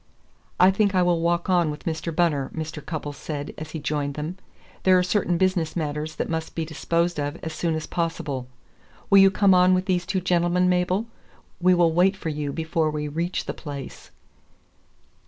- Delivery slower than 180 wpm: No, average, 190 wpm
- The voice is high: No, medium, 170 Hz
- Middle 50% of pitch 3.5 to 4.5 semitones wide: No, average, 2.9 semitones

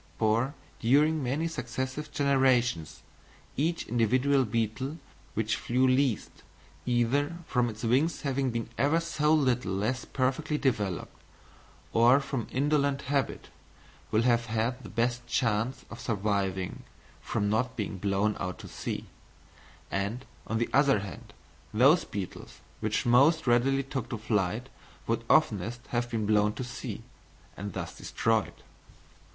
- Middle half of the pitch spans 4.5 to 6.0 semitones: No, average, 3.9 semitones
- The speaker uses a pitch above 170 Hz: No, low, 120 Hz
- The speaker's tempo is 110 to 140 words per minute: Yes, slow, 135 wpm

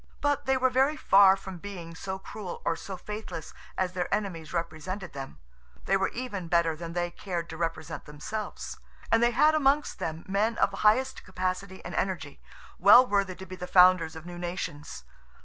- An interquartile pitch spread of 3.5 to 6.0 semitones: Yes, average, 4.0 semitones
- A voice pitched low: No, medium, 185 Hz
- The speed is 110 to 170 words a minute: No, average, 185 wpm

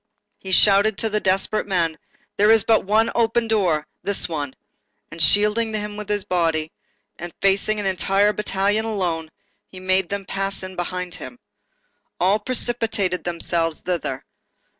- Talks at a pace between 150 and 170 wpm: No, average, 140 wpm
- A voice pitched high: Yes, high, 195 Hz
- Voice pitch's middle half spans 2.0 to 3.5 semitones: Yes, average, 3.2 semitones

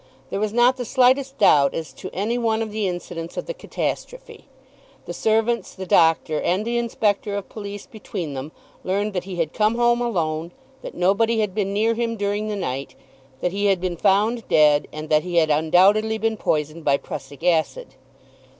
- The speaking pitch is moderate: No, high, 200 Hz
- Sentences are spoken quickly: No, average, 190 wpm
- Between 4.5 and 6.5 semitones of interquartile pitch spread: Yes, average, 5.1 semitones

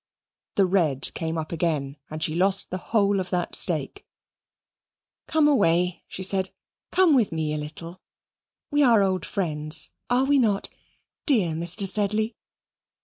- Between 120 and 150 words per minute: Yes, average, 145 wpm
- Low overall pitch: No, medium, 185 Hz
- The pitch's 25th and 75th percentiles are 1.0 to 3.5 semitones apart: No, average, 4.6 semitones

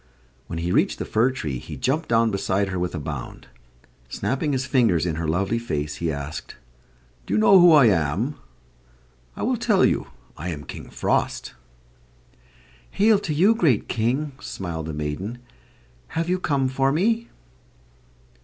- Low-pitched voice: Yes, low, 110 Hz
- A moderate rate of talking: Yes, average, 165 wpm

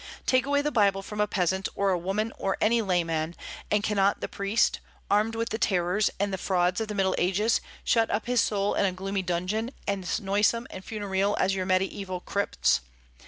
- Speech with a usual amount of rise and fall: No, narrow, 2.3 semitones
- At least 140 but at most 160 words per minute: No, average, 200 wpm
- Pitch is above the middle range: Yes, high, 200 Hz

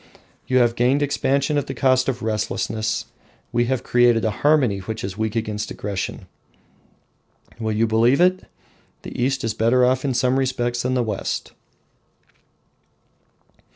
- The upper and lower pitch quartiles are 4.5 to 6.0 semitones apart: No, average, 2.9 semitones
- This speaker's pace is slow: No, average, 150 wpm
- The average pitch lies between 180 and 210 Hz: No, low, 120 Hz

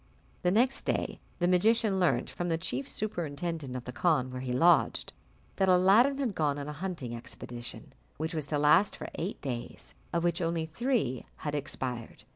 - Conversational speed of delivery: Yes, average, 180 wpm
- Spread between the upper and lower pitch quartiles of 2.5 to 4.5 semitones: No, average, 5.2 semitones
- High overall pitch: No, medium, 165 Hz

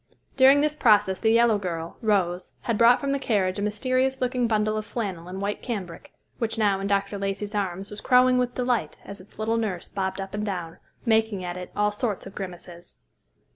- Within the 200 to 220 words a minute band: Yes, fast, 205 wpm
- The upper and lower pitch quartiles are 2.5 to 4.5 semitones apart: Yes, average, 3.5 semitones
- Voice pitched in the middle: No, high, 210 Hz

